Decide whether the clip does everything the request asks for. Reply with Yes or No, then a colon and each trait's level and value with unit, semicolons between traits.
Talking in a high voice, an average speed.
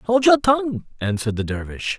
No: medium, 175 Hz; average, 180 wpm